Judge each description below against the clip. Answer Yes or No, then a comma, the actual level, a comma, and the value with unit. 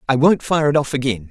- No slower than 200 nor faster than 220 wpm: No, fast, 275 wpm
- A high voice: No, low, 135 Hz